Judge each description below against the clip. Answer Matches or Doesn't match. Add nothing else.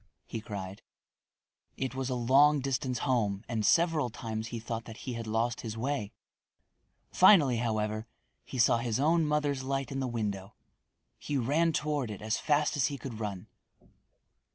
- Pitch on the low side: Matches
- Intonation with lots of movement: Doesn't match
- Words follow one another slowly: Doesn't match